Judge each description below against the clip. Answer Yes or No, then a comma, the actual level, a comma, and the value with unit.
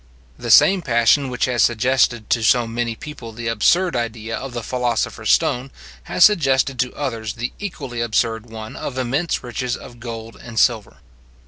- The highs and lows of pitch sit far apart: No, narrow, 2.5 semitones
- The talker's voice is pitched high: No, low, 120 Hz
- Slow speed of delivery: No, average, 175 wpm